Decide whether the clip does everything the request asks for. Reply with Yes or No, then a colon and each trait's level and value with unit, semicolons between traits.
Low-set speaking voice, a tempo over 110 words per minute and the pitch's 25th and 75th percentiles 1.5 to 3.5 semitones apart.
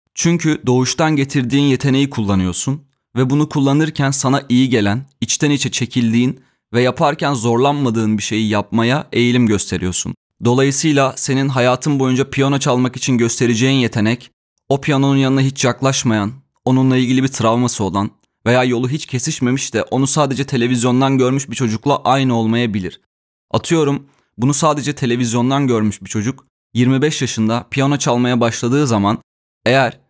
Yes: low, 130 Hz; average, 135 wpm; average, 2.7 semitones